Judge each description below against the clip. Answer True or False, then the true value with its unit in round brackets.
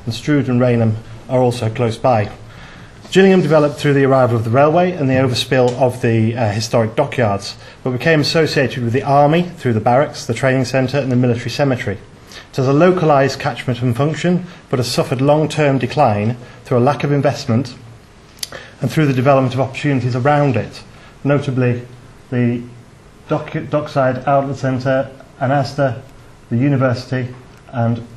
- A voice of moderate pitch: False (130 Hz)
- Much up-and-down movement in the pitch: False (2.9 semitones)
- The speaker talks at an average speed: True (160 wpm)